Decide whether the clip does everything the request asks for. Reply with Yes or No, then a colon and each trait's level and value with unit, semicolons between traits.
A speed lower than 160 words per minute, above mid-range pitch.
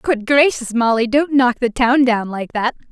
No: fast, 205 wpm; very high, 250 Hz